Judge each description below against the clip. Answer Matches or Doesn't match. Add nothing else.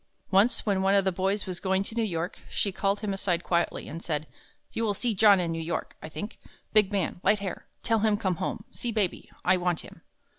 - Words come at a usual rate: Doesn't match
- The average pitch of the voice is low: Doesn't match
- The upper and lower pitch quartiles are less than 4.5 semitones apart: Matches